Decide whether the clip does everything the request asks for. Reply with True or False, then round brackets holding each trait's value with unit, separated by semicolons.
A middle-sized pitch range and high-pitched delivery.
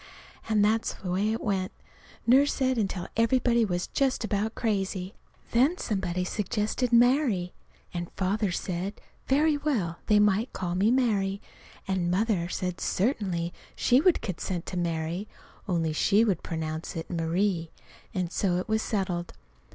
True (4.2 semitones; 195 Hz)